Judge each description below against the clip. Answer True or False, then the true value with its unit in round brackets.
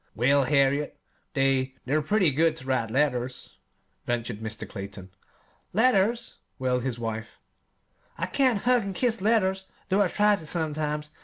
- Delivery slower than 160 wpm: True (150 wpm)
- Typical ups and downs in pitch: False (7.5 semitones)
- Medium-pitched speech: True (150 Hz)